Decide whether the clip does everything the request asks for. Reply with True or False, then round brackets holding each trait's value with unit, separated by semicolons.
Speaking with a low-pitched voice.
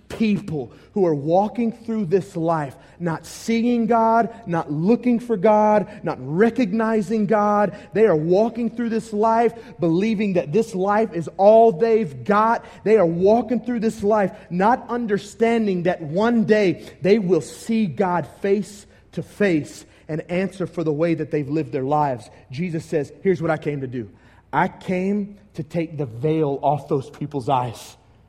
False (195 Hz)